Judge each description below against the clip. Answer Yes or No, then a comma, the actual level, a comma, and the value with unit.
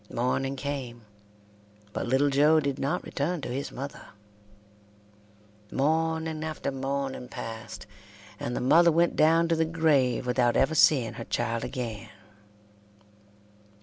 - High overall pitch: No, medium, 140 Hz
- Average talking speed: No, slow, 125 wpm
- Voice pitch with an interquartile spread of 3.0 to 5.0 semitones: Yes, average, 4.1 semitones